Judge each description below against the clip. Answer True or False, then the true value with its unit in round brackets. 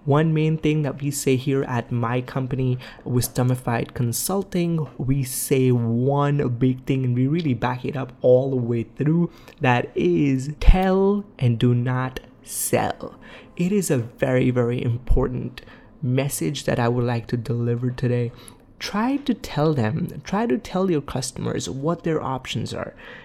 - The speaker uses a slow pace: False (160 wpm)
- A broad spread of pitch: False (3.9 semitones)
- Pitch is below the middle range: True (130 Hz)